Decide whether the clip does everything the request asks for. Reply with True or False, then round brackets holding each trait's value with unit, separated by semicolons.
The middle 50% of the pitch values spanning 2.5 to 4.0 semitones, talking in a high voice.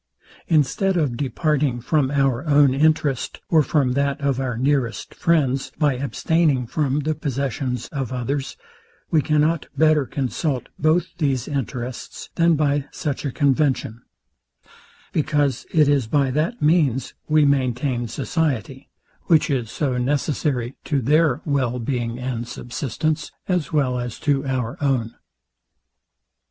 False (3.1 semitones; 140 Hz)